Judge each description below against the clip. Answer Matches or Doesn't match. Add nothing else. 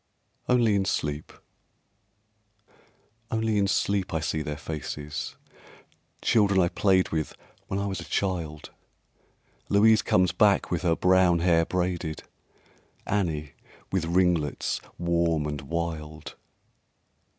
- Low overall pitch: Matches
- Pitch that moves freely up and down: Doesn't match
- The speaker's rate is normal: Doesn't match